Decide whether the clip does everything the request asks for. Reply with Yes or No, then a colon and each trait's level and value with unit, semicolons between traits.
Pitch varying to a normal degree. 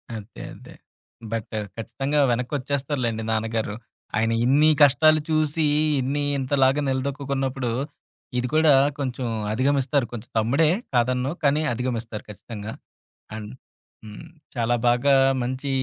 Yes: average, 3.6 semitones